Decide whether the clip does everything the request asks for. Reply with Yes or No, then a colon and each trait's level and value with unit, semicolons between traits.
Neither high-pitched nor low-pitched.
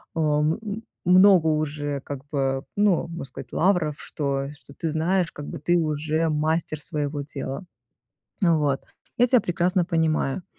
Yes: medium, 155 Hz